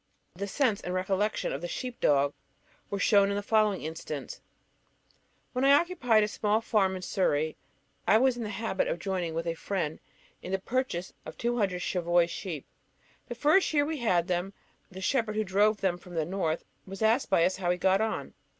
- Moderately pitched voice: No, high, 195 Hz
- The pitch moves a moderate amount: Yes, average, 4.0 semitones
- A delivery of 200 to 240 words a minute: Yes, fast, 205 wpm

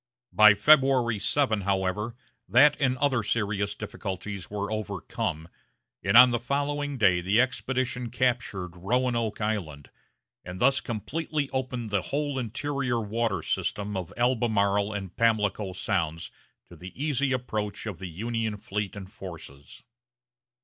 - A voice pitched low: Yes, low, 110 Hz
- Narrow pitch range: No, average, 4.2 semitones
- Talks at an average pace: No, slow, 130 wpm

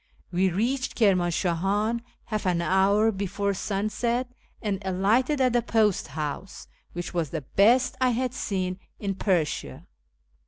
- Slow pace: Yes, slow, 130 wpm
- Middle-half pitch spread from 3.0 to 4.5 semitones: Yes, average, 4.1 semitones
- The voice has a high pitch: Yes, high, 200 Hz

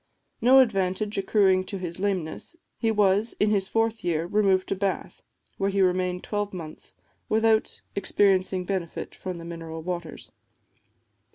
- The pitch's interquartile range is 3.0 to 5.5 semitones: No, narrow, 2.4 semitones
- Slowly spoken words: No, average, 145 wpm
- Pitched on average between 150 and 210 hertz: Yes, high, 190 Hz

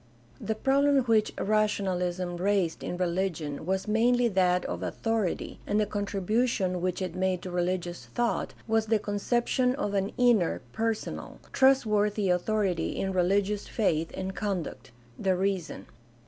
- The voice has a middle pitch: No, high, 195 Hz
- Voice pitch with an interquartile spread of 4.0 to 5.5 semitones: No, average, 3.3 semitones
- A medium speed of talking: Yes, average, 145 wpm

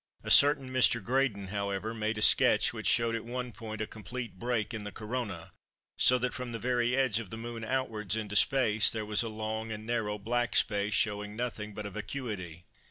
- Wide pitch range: No, average, 2.7 semitones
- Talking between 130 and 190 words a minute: No, fast, 205 wpm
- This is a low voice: Yes, low, 110 Hz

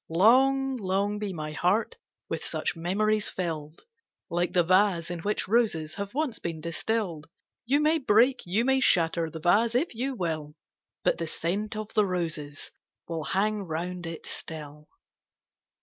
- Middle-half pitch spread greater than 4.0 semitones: Yes, average, 5.0 semitones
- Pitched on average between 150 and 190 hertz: Yes, medium, 185 Hz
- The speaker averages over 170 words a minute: No, average, 160 wpm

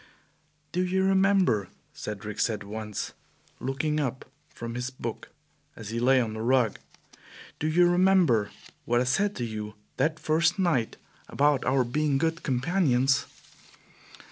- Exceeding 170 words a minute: No, average, 140 wpm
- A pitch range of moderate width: No, wide, 6.2 semitones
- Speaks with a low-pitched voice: Yes, low, 130 Hz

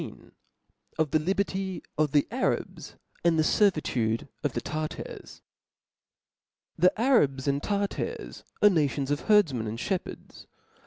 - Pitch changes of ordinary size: No, wide, 5.7 semitones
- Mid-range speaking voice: Yes, medium, 155 Hz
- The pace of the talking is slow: No, average, 145 wpm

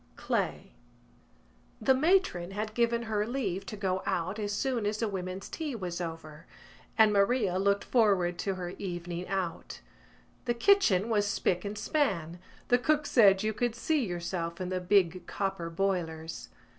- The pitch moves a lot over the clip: No, average, 4.2 semitones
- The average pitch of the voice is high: Yes, high, 195 Hz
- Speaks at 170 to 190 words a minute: No, average, 155 wpm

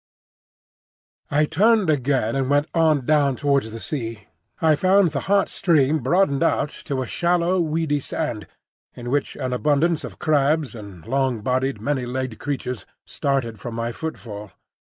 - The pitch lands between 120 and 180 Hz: Yes, medium, 140 Hz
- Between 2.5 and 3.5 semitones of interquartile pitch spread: No, average, 4.2 semitones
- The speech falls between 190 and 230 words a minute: No, average, 150 wpm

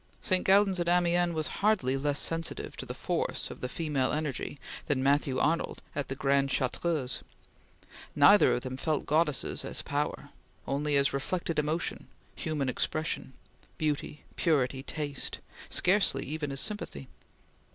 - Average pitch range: Yes, average, 3.5 semitones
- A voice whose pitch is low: No, medium, 150 Hz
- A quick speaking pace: No, average, 140 wpm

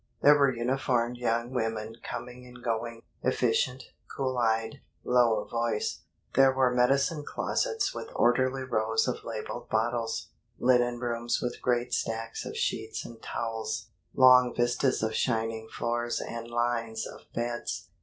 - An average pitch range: No, narrow, 1.8 semitones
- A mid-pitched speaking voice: No, low, 120 Hz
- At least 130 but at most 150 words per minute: Yes, average, 140 wpm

